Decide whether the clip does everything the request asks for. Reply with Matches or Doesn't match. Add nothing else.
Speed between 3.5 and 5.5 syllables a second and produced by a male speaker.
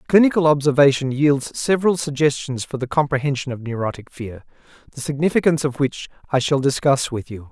Doesn't match